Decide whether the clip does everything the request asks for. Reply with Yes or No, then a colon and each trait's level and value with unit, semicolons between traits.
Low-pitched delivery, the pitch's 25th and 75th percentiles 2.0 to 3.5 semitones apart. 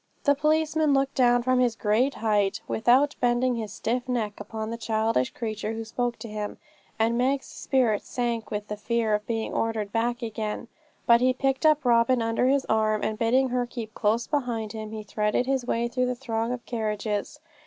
No: high, 235 Hz; narrow, 2.6 semitones